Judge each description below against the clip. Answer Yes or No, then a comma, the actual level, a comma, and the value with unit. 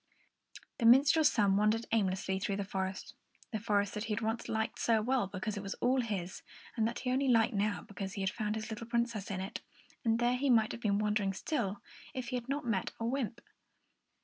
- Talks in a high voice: Yes, high, 220 Hz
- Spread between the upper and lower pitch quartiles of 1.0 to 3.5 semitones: Yes, average, 3.0 semitones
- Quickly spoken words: Yes, fast, 225 wpm